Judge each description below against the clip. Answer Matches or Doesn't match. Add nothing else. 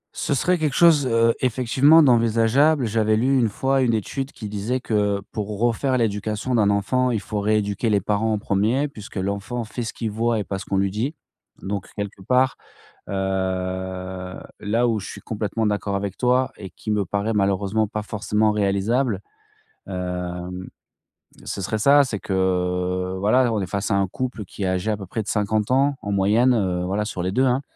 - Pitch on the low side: Matches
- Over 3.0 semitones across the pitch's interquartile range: Matches